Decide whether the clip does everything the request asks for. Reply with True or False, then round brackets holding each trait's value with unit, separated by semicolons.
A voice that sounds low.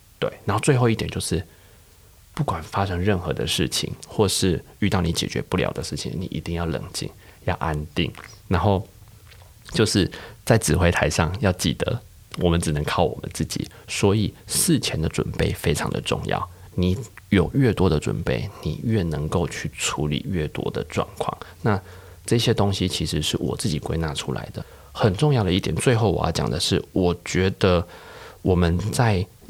True (95 Hz)